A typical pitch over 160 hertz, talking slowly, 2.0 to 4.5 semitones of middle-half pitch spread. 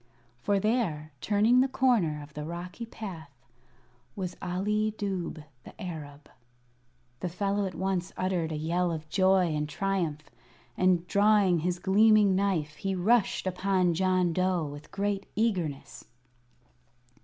Yes: medium, 185 Hz; slow, 130 wpm; average, 3.5 semitones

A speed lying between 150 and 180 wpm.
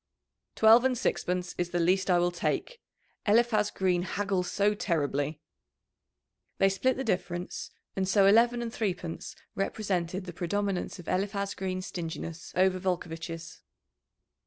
No: slow, 135 wpm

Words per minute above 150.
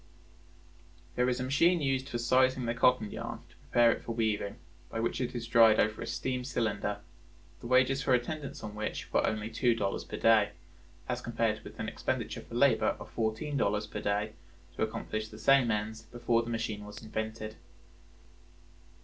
Yes: average, 185 wpm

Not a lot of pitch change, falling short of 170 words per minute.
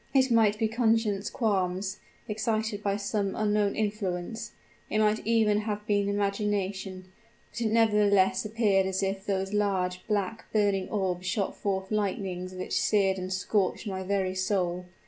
Yes: narrow, 1.9 semitones; average, 145 wpm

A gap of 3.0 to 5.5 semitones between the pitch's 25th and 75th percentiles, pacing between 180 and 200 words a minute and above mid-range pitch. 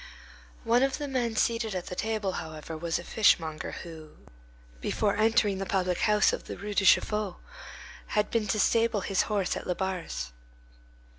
No: average, 3.9 semitones; average, 165 wpm; high, 200 Hz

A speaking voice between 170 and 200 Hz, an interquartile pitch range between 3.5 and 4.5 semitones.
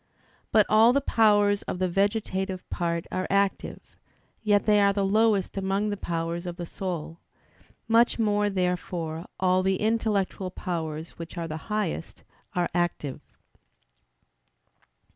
No: high, 190 Hz; average, 3.1 semitones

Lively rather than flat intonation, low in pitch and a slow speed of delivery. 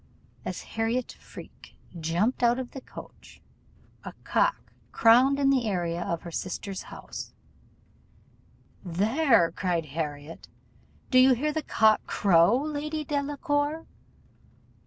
No: wide, 8.3 semitones; high, 235 Hz; slow, 115 wpm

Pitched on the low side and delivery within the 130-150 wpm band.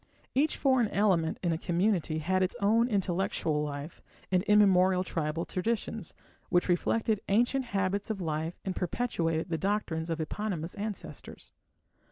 No: medium, 185 Hz; average, 140 wpm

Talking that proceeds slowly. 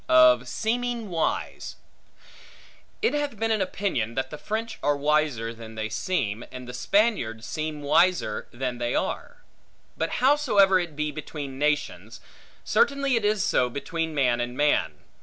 No: average, 150 wpm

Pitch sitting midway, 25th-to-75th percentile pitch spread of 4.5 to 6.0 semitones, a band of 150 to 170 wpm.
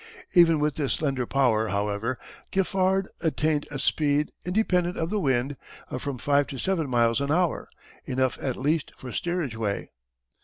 Yes: medium, 145 Hz; average, 5.0 semitones; average, 160 wpm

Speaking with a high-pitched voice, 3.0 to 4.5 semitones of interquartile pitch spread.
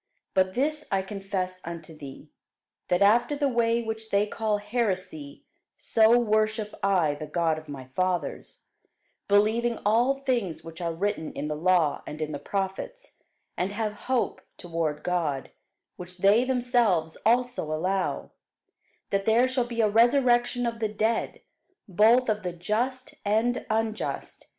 No: high, 205 Hz; average, 5.0 semitones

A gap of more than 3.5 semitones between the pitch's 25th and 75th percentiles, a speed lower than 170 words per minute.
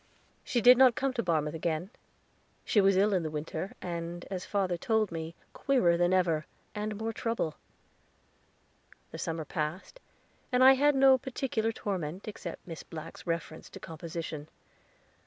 Yes: wide, 5.5 semitones; average, 150 wpm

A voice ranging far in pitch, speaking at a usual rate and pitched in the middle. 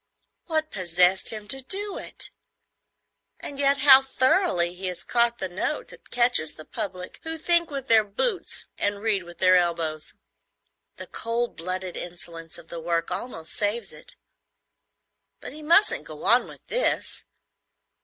No: wide, 7.6 semitones; average, 155 wpm; high, 210 Hz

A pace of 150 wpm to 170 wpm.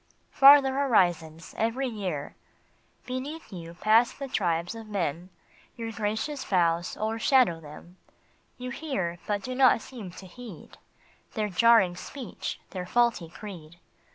Yes: average, 155 wpm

